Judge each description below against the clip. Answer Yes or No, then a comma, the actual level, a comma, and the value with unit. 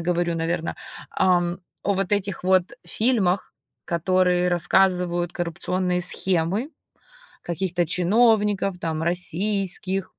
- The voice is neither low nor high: Yes, medium, 180 Hz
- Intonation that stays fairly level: Yes, narrow, 1.8 semitones